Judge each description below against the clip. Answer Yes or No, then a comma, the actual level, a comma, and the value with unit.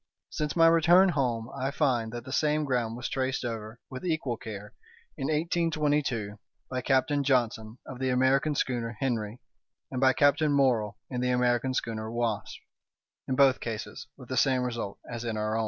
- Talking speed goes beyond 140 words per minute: Yes, average, 170 wpm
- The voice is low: Yes, low, 125 Hz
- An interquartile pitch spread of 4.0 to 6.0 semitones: No, average, 3.4 semitones